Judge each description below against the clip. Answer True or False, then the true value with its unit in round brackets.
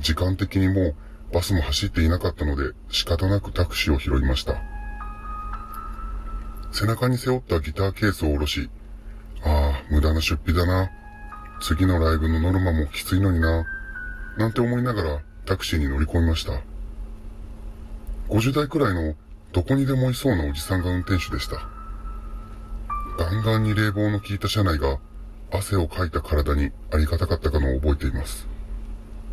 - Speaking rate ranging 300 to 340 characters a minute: True (320 characters per minute)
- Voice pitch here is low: True (85 Hz)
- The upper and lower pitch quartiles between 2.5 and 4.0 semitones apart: False (5.6 semitones)